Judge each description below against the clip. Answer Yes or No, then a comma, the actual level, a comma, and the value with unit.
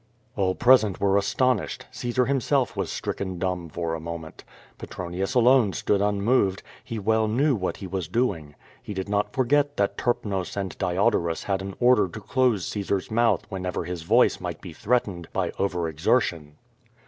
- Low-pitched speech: Yes, low, 100 Hz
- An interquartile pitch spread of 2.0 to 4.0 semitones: No, average, 4.6 semitones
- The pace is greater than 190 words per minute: No, average, 170 wpm